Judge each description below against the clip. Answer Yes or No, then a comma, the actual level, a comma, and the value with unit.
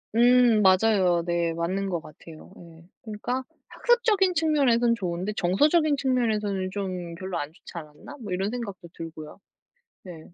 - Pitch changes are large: Yes, wide, 6.0 semitones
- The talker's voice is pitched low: No, high, 195 Hz